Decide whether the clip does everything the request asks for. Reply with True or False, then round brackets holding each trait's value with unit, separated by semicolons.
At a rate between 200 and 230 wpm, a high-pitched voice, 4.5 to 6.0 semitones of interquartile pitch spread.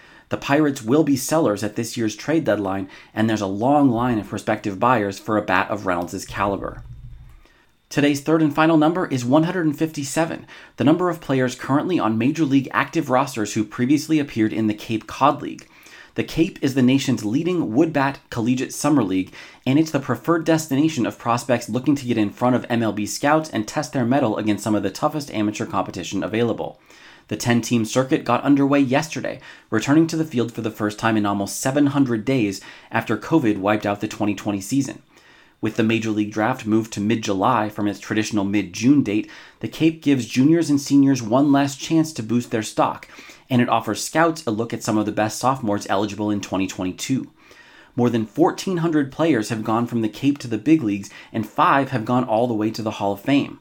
False (205 wpm; 120 Hz; 4.9 semitones)